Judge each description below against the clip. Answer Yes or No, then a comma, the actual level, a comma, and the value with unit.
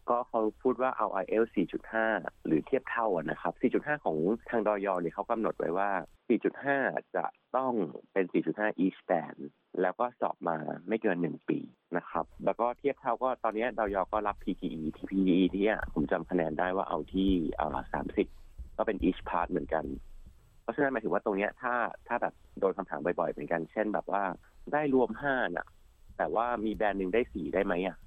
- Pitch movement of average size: Yes, average, 4.1 semitones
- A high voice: No, low, 105 Hz